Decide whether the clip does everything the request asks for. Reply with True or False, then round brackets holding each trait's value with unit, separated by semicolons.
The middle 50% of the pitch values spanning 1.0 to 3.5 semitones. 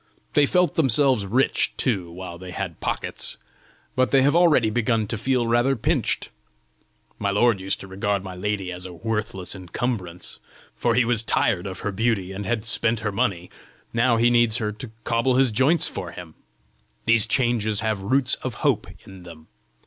False (4.1 semitones)